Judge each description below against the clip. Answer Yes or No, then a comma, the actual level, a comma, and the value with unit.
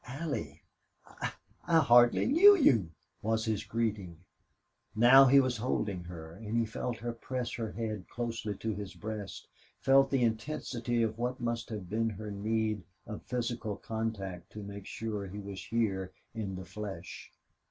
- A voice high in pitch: No, low, 110 Hz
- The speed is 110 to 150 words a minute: No, average, 160 wpm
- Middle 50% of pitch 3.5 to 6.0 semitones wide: No, average, 3.0 semitones